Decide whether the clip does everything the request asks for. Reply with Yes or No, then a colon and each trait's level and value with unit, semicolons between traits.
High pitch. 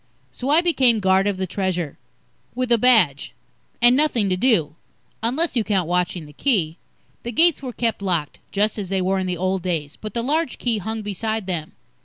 Yes: high, 205 Hz